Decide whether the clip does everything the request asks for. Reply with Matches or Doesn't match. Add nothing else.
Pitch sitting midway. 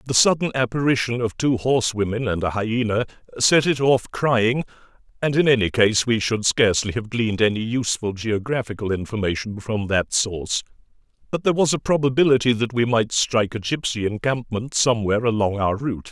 Doesn't match